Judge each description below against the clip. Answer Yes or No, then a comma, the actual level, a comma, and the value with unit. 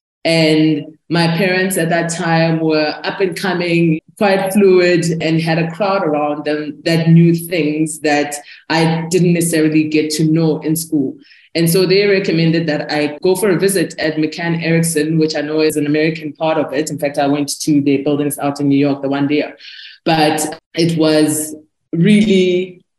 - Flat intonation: Yes, narrow, 2.0 semitones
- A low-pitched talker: No, medium, 160 Hz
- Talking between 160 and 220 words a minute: Yes, average, 185 wpm